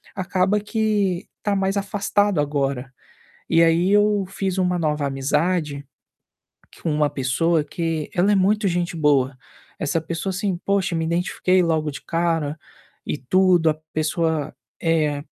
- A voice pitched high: No, medium, 170 Hz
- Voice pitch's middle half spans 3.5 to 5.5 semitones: Yes, average, 4.1 semitones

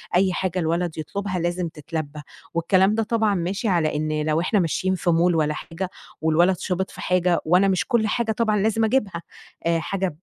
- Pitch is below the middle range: No, medium, 180 Hz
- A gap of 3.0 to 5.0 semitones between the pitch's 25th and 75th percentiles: Yes, average, 3.3 semitones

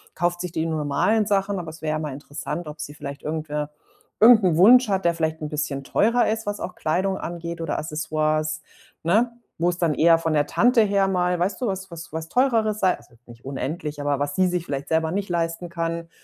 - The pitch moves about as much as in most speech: Yes, average, 3.8 semitones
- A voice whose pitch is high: No, medium, 165 Hz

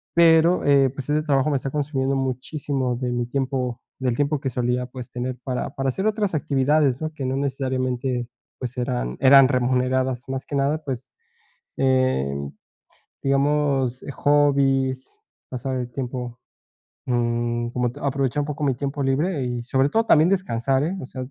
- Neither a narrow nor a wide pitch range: No, narrow, 2.3 semitones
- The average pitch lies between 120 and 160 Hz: Yes, low, 135 Hz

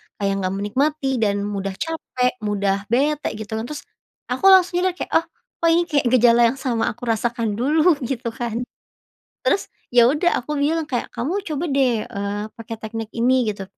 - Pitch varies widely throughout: Yes, wide, 5.7 semitones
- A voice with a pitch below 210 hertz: No, high, 245 Hz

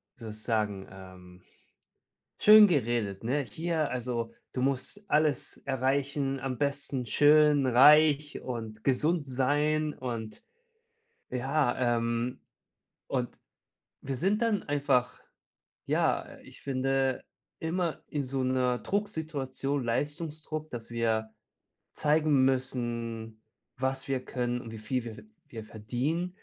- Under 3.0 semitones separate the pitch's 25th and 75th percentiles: No, average, 3.8 semitones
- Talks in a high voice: No, low, 130 Hz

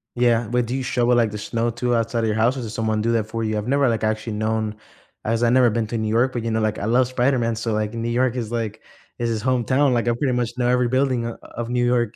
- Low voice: Yes, low, 115 Hz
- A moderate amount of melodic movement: No, narrow, 1.9 semitones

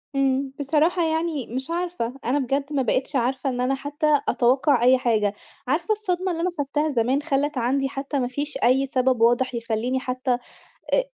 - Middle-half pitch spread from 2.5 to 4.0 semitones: Yes, average, 2.9 semitones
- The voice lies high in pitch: Yes, very high, 270 Hz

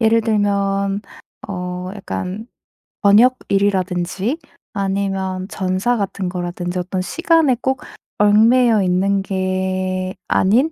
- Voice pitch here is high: Yes, high, 195 Hz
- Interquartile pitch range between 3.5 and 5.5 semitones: No, narrow, 2.6 semitones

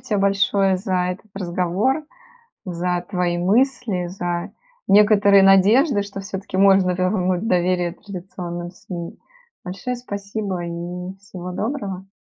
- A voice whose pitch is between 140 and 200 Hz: Yes, high, 190 Hz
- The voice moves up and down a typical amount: No, narrow, 2.1 semitones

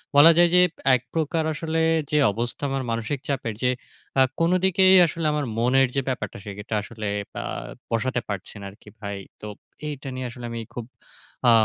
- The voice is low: Yes, low, 130 Hz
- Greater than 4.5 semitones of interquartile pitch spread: Yes, average, 4.9 semitones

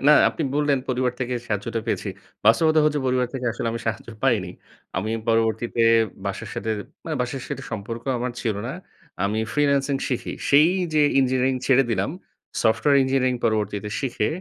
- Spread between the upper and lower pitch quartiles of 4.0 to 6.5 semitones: No, average, 3.5 semitones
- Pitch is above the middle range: No, low, 125 Hz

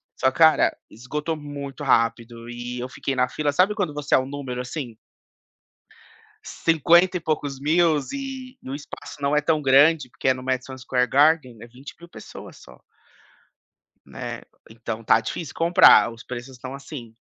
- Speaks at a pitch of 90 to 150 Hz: Yes, medium, 140 Hz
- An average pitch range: Yes, average, 3.9 semitones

